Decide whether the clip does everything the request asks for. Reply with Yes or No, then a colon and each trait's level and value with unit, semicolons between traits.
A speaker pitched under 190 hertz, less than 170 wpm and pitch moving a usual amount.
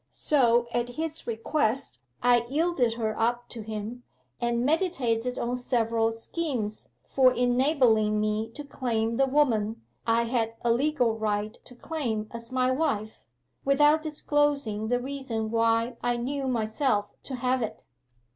No: high, 240 Hz; average, 140 wpm; average, 3.3 semitones